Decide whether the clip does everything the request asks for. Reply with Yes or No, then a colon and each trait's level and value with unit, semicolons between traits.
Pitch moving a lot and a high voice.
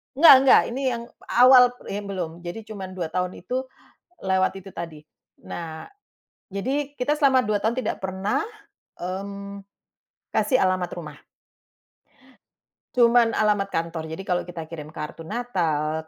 Yes: wide, 5.7 semitones; high, 195 Hz